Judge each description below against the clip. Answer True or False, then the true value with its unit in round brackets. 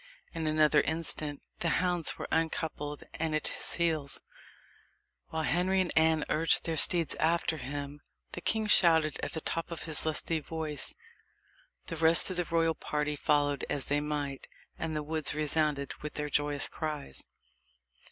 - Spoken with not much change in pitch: True (1.8 semitones)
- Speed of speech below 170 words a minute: True (160 wpm)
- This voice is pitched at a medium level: True (155 Hz)